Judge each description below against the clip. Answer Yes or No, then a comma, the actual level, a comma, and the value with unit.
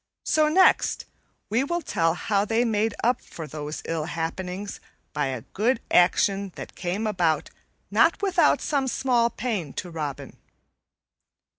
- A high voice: Yes, high, 200 Hz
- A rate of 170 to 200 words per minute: No, average, 140 wpm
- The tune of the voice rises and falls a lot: Yes, wide, 6.3 semitones